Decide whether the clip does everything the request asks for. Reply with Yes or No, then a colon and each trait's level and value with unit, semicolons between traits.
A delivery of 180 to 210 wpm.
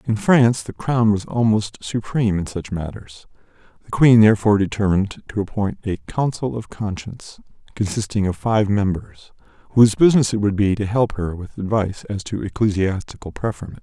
No: average, 165 wpm